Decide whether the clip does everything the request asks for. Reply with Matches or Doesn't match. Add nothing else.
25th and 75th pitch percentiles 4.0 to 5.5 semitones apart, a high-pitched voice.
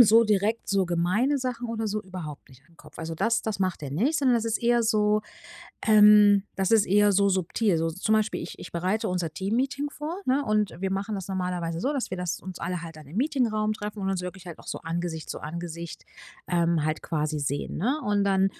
Matches